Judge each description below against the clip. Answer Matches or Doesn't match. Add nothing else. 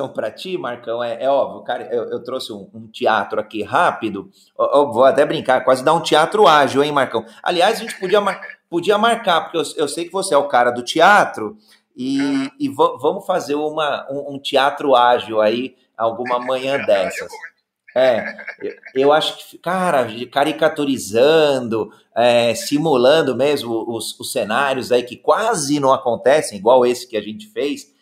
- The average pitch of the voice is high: Doesn't match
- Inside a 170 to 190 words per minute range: Matches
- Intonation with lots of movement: Matches